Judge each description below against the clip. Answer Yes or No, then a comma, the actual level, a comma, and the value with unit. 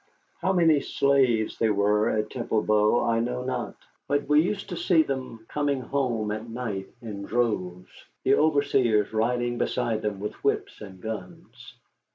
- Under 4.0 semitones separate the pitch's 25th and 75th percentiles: No, average, 4.6 semitones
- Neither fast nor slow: Yes, average, 160 wpm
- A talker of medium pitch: No, low, 115 Hz